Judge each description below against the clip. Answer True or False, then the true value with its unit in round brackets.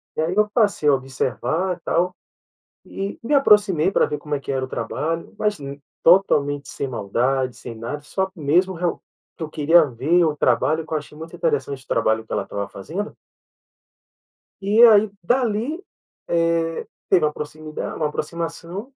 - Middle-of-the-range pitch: True (160 Hz)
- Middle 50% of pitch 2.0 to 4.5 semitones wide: False (5.3 semitones)